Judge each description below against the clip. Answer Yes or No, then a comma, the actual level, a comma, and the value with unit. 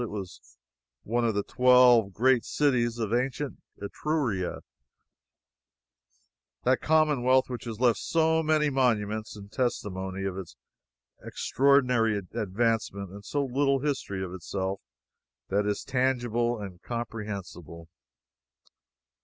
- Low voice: Yes, low, 115 Hz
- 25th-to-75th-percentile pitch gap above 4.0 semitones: Yes, average, 4.5 semitones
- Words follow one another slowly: Yes, slow, 110 wpm